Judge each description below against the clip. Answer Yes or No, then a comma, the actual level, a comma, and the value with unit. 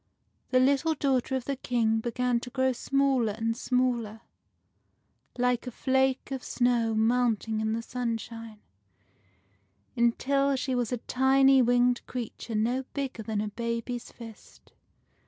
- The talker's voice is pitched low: No, high, 245 Hz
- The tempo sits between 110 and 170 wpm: Yes, slow, 135 wpm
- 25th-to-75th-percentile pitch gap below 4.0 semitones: Yes, narrow, 2.4 semitones